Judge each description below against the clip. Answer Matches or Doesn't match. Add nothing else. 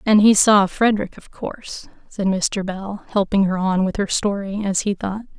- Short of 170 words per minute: Doesn't match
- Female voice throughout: Matches